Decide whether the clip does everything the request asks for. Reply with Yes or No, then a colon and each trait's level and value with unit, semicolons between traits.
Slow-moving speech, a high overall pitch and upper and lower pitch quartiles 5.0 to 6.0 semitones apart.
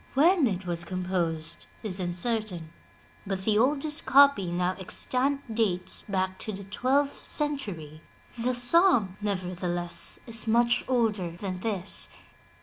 Yes: slow, 125 wpm; high, 200 Hz; wide, 5.4 semitones